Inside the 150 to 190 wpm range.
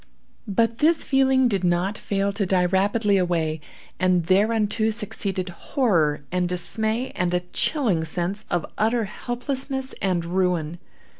No: slow, 135 wpm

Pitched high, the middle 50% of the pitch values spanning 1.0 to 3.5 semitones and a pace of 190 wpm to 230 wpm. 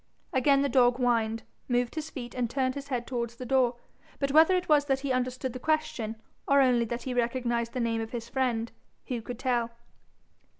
Yes: very high, 250 Hz; narrow, 2.4 semitones; fast, 205 wpm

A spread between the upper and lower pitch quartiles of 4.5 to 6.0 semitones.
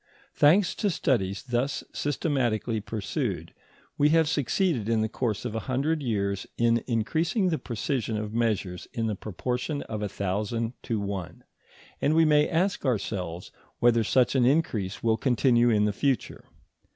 Yes: average, 5.2 semitones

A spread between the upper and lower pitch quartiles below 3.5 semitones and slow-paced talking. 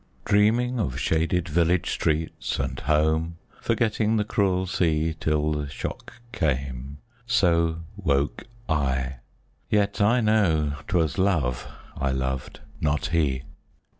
No: wide, 5.5 semitones; slow, 115 wpm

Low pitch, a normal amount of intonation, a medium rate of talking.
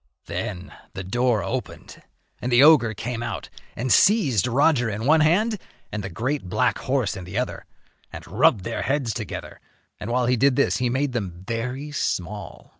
Yes: low, 120 Hz; average, 4.6 semitones; average, 180 wpm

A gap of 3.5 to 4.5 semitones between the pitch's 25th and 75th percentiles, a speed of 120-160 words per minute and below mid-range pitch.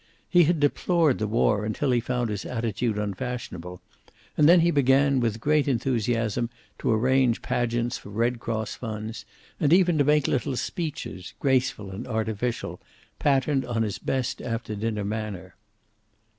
Yes: average, 3.8 semitones; average, 150 wpm; low, 120 Hz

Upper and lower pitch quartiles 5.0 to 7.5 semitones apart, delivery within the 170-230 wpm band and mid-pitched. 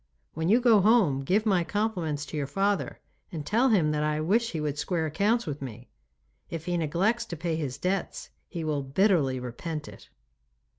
Yes: average, 5.3 semitones; average, 190 wpm; medium, 165 Hz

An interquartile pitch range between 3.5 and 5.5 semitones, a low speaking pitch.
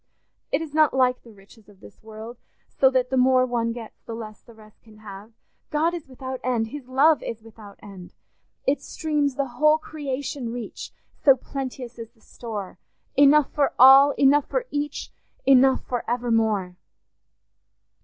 No: average, 3.8 semitones; very high, 255 Hz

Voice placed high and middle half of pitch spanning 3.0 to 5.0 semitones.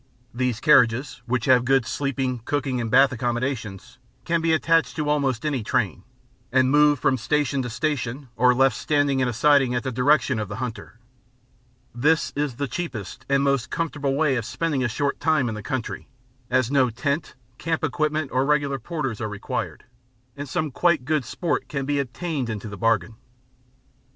No: low, 135 Hz; average, 3.3 semitones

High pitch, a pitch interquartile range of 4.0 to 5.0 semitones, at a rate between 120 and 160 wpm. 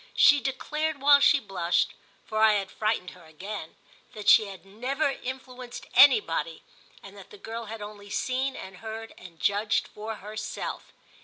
Yes: high, 220 Hz; average, 4.6 semitones; average, 150 wpm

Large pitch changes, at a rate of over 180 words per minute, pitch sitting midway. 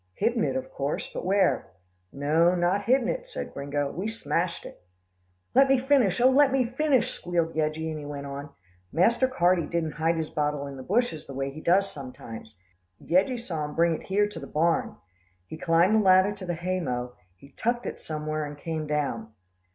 Yes: wide, 6.2 semitones; average, 200 wpm; medium, 170 Hz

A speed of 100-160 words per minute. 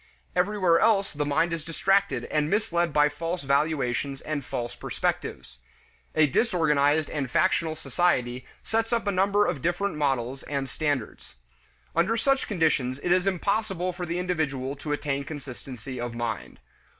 Yes: average, 150 wpm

